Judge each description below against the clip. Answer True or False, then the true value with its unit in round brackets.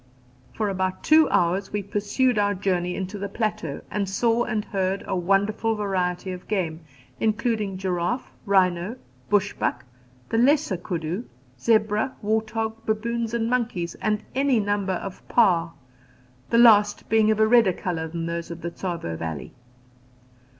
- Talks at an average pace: True (150 wpm)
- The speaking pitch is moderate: False (205 Hz)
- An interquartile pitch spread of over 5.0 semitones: False (3.6 semitones)